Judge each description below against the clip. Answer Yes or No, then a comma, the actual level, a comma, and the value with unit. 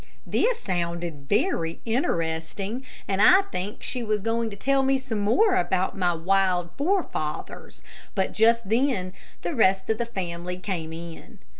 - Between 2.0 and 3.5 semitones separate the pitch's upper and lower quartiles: No, average, 5.0 semitones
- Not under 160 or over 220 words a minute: No, average, 150 wpm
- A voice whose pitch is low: No, high, 195 Hz